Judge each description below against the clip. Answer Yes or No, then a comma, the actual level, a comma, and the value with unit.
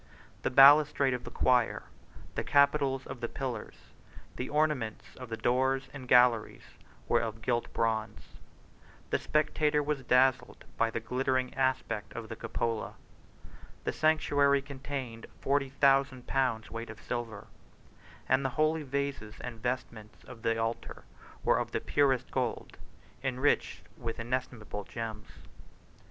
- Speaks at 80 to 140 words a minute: Yes, slow, 135 wpm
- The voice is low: Yes, low, 130 Hz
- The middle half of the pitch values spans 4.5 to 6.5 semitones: No, average, 3.1 semitones